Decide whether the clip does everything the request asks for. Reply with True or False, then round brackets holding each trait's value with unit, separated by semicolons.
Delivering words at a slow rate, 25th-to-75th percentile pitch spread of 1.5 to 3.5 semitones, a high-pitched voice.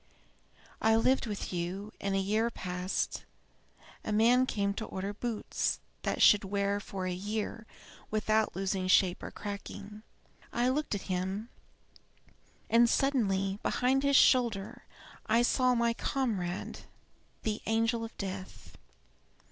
True (130 wpm; 3.2 semitones; 210 Hz)